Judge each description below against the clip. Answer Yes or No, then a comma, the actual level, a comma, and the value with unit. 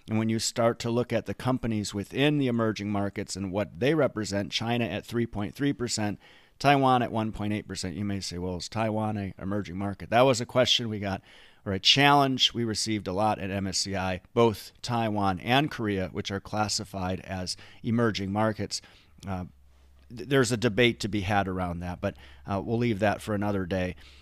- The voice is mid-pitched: No, low, 105 Hz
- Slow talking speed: No, average, 185 wpm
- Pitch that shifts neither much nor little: Yes, average, 3.2 semitones